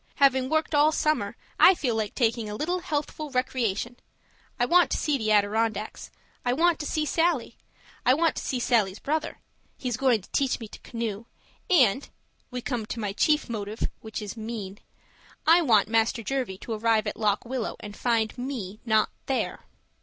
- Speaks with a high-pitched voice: Yes, high, 240 Hz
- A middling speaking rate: Yes, average, 180 wpm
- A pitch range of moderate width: Yes, average, 4.7 semitones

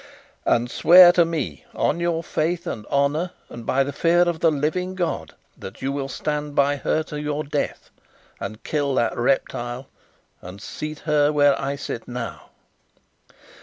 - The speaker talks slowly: No, average, 165 wpm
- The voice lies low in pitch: No, medium, 145 Hz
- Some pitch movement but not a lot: Yes, average, 3.5 semitones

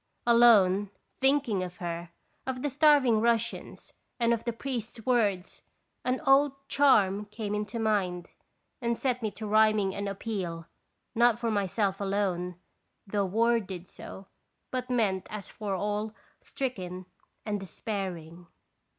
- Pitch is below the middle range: No, high, 210 Hz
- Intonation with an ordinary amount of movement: Yes, average, 3.7 semitones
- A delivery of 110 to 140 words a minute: Yes, slow, 135 wpm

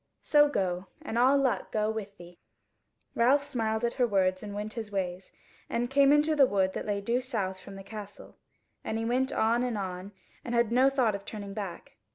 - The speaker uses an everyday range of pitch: Yes, average, 4.0 semitones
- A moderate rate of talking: No, fast, 210 wpm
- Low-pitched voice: No, high, 220 Hz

